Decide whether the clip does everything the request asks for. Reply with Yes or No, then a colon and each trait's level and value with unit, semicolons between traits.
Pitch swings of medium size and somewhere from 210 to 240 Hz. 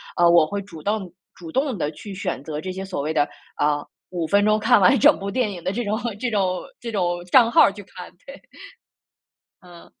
No: average, 3.7 semitones; high, 190 Hz